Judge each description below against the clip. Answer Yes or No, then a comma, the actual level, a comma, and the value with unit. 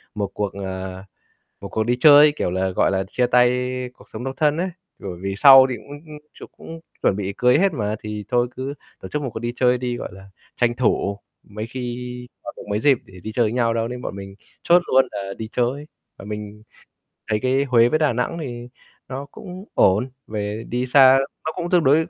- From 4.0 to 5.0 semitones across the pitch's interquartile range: Yes, average, 4.3 semitones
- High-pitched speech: No, low, 120 Hz